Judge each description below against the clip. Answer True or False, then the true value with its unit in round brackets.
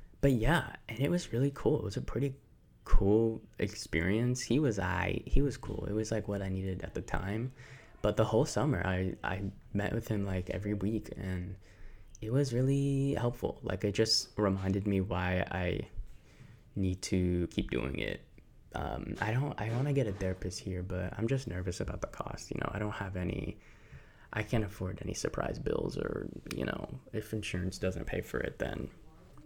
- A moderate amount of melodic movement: True (4.5 semitones)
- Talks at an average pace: True (195 wpm)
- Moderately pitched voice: False (105 Hz)